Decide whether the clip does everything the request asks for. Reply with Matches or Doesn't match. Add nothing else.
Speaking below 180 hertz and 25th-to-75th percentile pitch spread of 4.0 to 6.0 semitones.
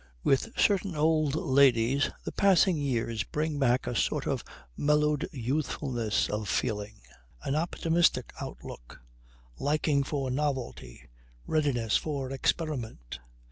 Matches